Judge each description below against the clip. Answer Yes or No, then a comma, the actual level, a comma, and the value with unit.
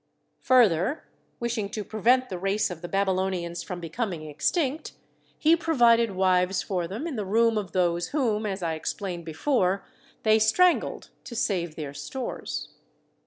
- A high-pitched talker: Yes, high, 200 Hz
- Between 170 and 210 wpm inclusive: No, average, 155 wpm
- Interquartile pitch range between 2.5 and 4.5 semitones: No, average, 5.0 semitones